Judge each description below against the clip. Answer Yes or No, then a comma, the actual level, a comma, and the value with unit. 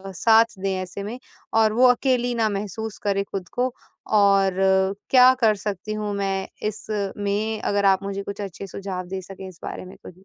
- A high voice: Yes, high, 200 Hz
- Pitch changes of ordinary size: No, narrow, 2.2 semitones